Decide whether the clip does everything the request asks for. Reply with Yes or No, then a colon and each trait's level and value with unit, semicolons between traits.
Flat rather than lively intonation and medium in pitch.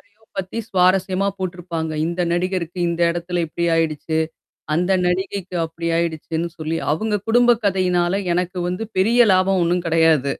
Yes: narrow, 2.2 semitones; medium, 180 Hz